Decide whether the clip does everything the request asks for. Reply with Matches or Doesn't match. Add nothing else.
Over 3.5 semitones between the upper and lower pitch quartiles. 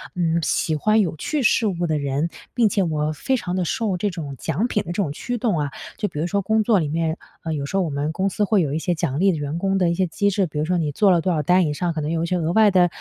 Matches